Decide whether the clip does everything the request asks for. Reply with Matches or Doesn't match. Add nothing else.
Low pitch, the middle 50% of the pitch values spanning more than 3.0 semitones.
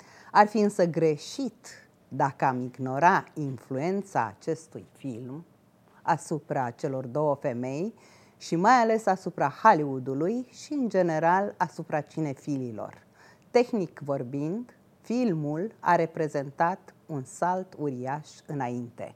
Doesn't match